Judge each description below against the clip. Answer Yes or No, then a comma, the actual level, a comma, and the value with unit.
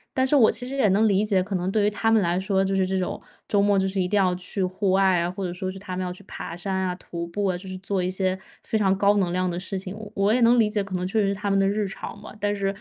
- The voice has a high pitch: Yes, high, 195 Hz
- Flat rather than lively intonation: Yes, narrow, 1.8 semitones